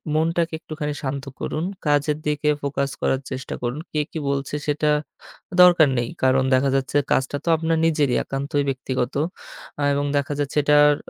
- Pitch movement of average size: No, narrow, 2.1 semitones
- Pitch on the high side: No, medium, 145 Hz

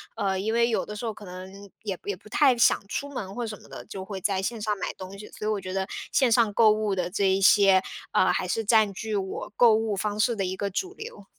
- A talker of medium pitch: No, high, 210 Hz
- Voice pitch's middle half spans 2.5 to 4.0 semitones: Yes, average, 2.8 semitones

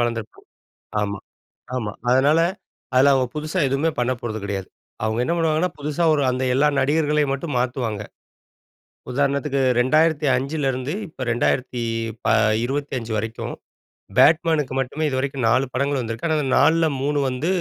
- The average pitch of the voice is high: No, low, 135 Hz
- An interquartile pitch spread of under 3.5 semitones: No, average, 3.8 semitones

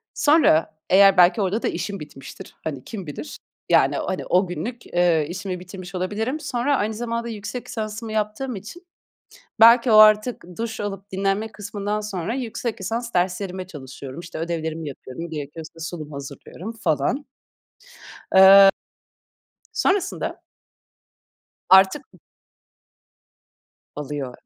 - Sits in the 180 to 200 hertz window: Yes, high, 195 Hz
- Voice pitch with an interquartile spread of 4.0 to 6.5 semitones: Yes, average, 4.8 semitones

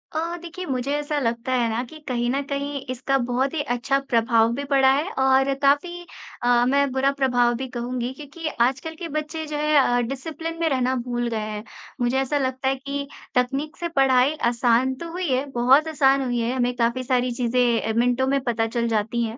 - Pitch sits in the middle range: No, very high, 260 Hz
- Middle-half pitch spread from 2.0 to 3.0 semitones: Yes, average, 2.7 semitones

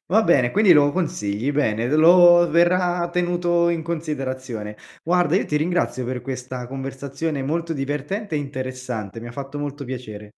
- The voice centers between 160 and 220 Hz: No, medium, 145 Hz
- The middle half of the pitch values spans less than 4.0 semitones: No, average, 5.0 semitones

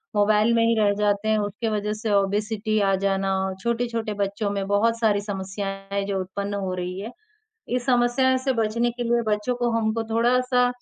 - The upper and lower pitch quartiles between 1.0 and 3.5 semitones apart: Yes, average, 2.7 semitones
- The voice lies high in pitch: Yes, high, 215 Hz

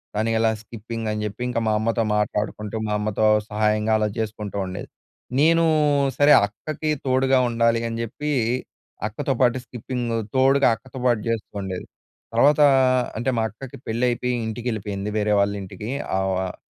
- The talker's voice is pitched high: No, low, 115 Hz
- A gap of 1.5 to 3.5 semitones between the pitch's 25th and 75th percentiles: Yes, average, 2.9 semitones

